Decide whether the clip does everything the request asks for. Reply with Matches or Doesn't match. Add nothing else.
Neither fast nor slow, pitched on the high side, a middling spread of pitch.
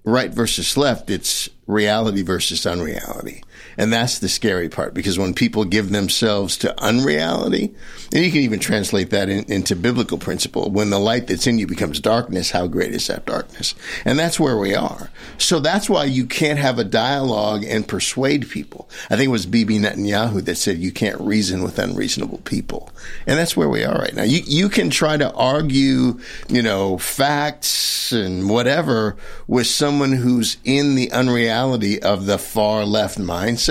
Doesn't match